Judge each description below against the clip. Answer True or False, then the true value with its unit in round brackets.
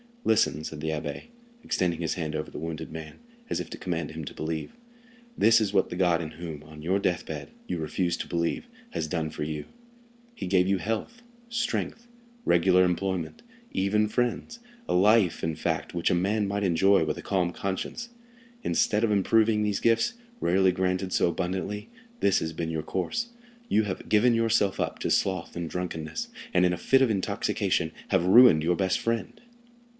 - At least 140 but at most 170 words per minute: False (180 wpm)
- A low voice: True (95 Hz)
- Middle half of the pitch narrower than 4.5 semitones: False (4.8 semitones)